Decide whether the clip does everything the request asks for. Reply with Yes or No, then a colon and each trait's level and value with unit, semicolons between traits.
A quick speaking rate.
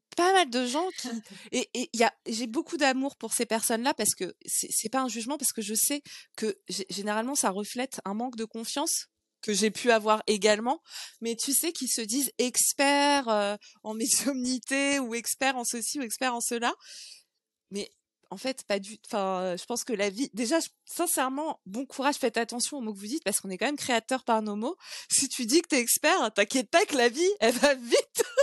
Yes: fast, 225 wpm